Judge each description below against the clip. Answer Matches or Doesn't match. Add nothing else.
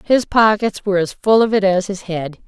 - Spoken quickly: Matches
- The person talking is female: Matches